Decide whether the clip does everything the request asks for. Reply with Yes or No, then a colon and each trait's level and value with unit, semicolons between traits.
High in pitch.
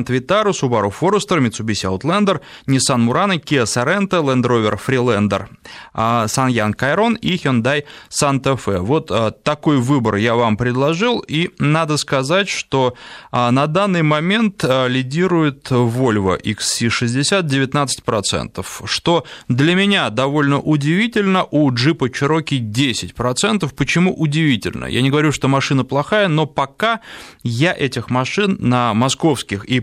No: medium, 140 Hz